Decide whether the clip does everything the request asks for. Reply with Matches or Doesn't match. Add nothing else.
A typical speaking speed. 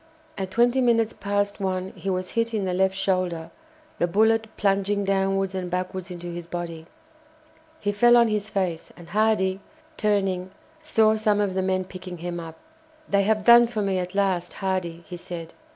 Matches